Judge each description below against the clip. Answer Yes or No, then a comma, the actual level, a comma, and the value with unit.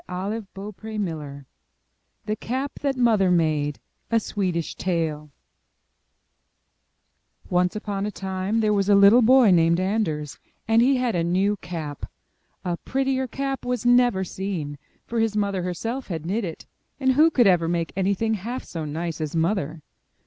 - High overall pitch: Yes, high, 195 Hz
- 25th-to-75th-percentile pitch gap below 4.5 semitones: No, average, 5.1 semitones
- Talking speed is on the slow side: No, average, 155 wpm